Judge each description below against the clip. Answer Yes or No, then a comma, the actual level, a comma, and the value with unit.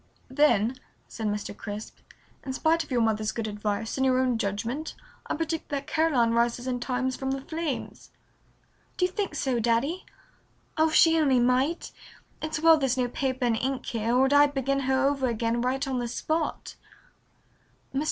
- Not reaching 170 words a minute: No, average, 180 wpm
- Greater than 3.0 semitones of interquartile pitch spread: Yes, average, 3.7 semitones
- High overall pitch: Yes, very high, 260 Hz